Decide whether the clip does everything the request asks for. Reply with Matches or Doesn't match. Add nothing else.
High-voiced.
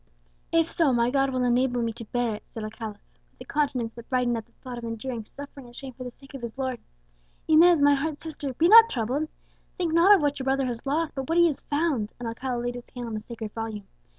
Matches